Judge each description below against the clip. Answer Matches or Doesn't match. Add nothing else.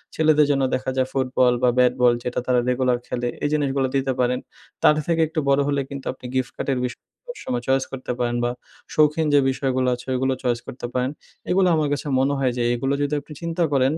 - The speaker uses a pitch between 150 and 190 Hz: Doesn't match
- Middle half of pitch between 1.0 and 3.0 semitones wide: Matches